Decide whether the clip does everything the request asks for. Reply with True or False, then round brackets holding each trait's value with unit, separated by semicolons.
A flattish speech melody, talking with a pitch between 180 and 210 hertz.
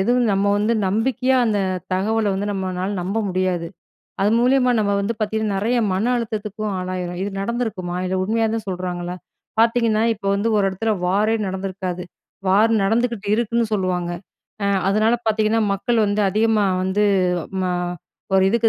False (3.1 semitones; 205 Hz)